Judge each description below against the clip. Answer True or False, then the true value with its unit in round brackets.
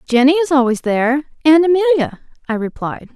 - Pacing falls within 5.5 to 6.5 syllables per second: True (6.0 syllables/s)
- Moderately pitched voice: False (280 Hz)